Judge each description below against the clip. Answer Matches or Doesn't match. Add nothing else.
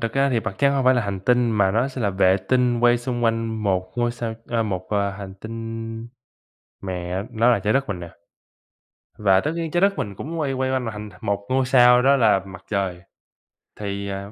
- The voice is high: Doesn't match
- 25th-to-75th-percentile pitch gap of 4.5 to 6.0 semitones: Doesn't match